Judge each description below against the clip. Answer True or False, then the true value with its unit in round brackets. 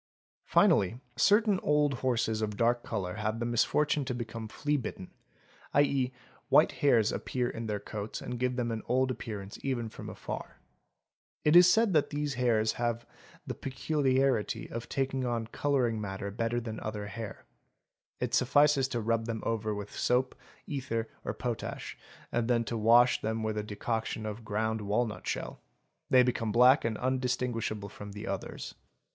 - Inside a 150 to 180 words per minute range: True (160 wpm)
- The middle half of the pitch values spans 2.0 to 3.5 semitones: True (3.0 semitones)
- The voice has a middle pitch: False (115 Hz)